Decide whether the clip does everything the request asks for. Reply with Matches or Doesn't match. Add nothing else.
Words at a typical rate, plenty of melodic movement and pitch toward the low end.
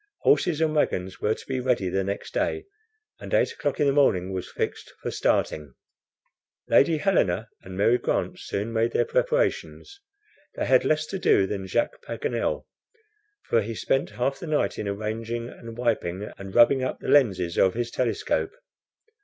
Matches